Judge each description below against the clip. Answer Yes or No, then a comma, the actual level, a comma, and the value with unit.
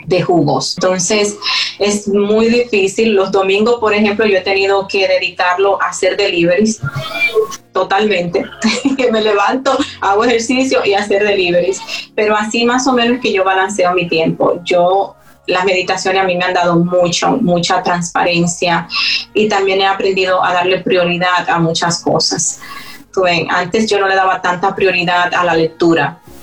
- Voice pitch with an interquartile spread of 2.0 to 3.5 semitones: Yes, average, 2.9 semitones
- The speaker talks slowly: No, average, 160 wpm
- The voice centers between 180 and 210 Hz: Yes, high, 190 Hz